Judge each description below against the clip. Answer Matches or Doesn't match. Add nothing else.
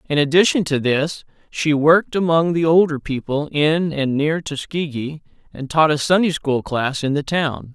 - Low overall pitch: Doesn't match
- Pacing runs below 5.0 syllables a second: Matches